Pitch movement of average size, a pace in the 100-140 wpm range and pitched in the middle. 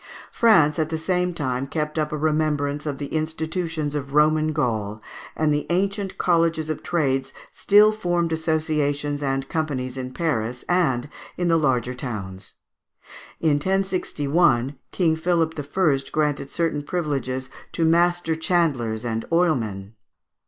Yes: average, 3.6 semitones; slow, 135 wpm; medium, 155 Hz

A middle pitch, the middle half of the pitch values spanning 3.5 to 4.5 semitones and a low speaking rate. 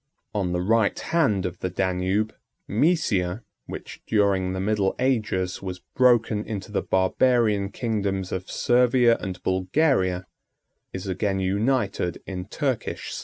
No: low, 100 Hz; average, 3.8 semitones; slow, 130 wpm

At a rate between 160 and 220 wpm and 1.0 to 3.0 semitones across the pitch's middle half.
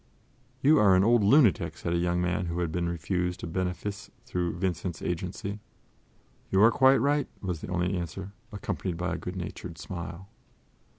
Yes: average, 175 wpm; narrow, 2.5 semitones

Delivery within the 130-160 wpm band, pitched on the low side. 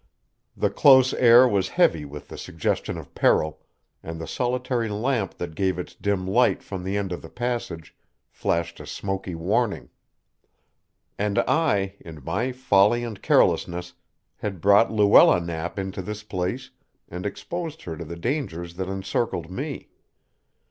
Yes: average, 150 wpm; very low, 95 Hz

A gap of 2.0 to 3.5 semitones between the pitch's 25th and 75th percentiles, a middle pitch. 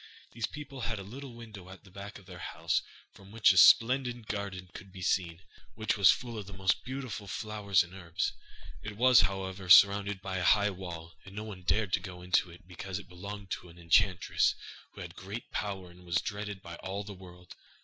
No: average, 2.7 semitones; very low, 95 Hz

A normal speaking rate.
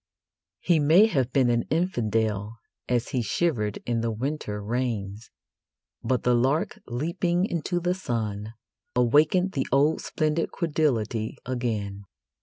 No: slow, 125 wpm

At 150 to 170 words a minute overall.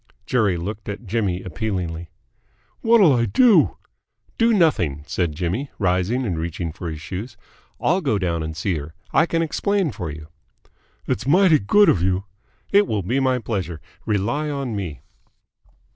Yes: average, 160 wpm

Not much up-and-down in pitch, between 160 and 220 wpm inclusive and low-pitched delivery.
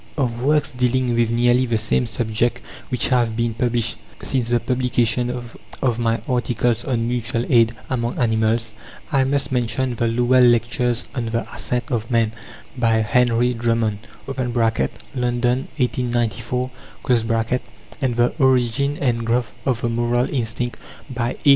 No: narrow, 1.4 semitones; average, 140 wpm; low, 120 Hz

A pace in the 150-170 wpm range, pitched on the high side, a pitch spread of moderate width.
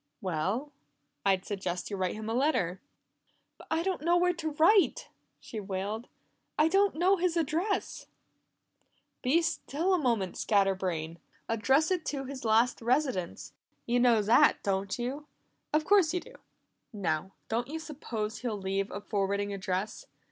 No: average, 155 wpm; high, 235 Hz; wide, 8.1 semitones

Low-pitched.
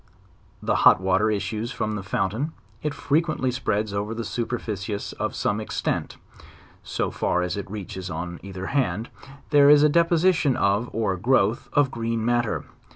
Yes: low, 110 Hz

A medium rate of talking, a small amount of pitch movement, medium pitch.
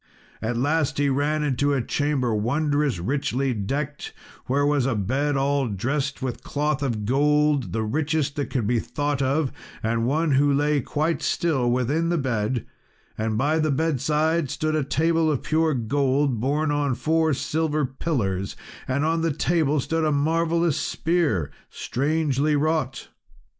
No: average, 155 wpm; average, 3.1 semitones; medium, 145 Hz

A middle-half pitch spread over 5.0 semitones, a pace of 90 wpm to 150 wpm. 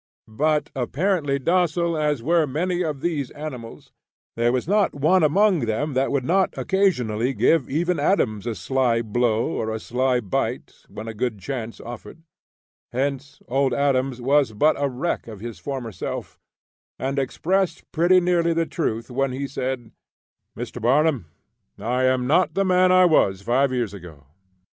No: wide, 5.5 semitones; average, 160 wpm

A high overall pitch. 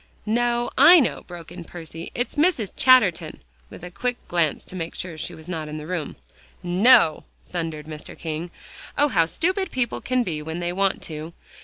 No: medium, 180 Hz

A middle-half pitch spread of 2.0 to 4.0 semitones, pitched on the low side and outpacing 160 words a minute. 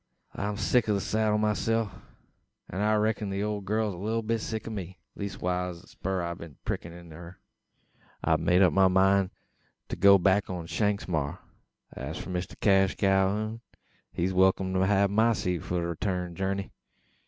Yes: average, 2.7 semitones; very low, 95 Hz; average, 190 wpm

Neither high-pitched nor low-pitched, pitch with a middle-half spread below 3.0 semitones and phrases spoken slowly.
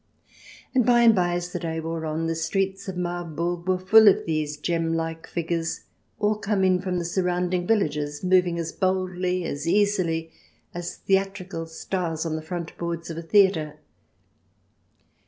No: medium, 175 Hz; narrow, 2.5 semitones; average, 165 wpm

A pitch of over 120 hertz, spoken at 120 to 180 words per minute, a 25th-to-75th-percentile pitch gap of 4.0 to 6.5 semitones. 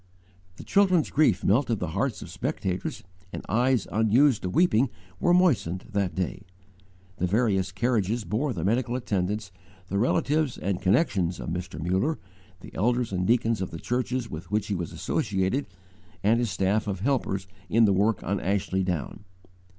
No: low, 105 Hz; average, 165 wpm; average, 4.6 semitones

